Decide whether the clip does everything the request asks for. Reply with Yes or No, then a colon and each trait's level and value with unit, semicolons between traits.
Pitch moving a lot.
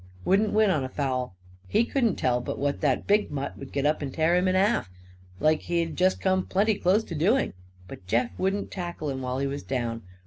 Yes: wide, 6.2 semitones